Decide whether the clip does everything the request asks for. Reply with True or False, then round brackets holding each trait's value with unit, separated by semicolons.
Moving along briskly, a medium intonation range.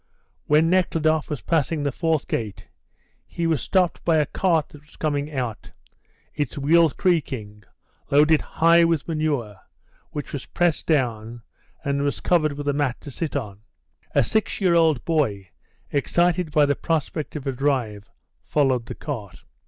False (160 wpm; 3.7 semitones)